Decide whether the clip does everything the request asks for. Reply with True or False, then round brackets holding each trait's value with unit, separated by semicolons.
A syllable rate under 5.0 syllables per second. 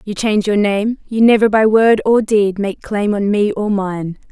True (4.5 syllables/s)